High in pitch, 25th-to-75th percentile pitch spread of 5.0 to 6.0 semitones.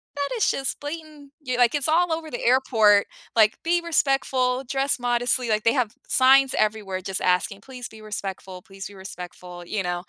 Yes: high, 245 Hz; average, 5.3 semitones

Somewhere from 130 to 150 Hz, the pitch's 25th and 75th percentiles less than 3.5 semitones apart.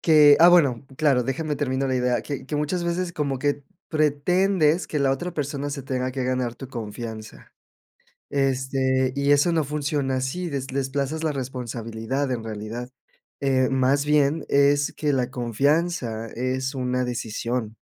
Yes: low, 135 Hz; average, 2.7 semitones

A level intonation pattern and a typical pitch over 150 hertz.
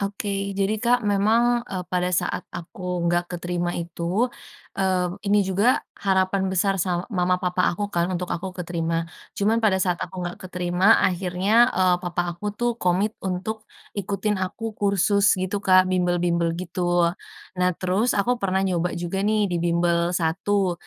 Yes: narrow, 2.1 semitones; medium, 185 Hz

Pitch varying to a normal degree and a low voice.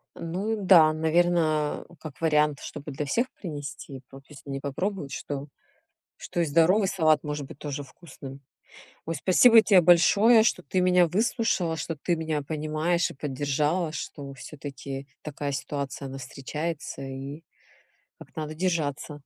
No: average, 3.7 semitones; medium, 155 Hz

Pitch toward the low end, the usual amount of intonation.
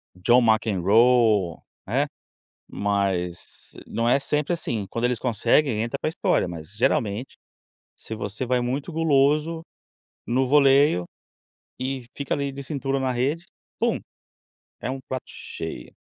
Yes: low, 125 Hz; average, 4.5 semitones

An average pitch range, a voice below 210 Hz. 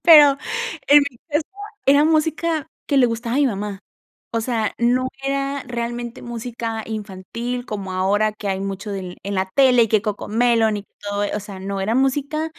No: average, 4.8 semitones; high, 230 Hz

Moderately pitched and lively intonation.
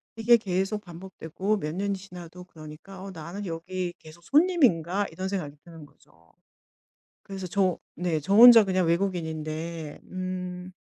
No: medium, 180 Hz; average, 3.1 semitones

